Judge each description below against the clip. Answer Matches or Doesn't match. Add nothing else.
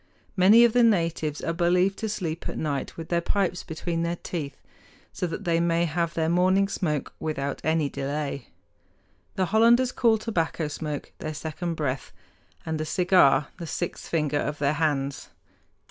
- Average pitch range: Matches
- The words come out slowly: Doesn't match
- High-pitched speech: Doesn't match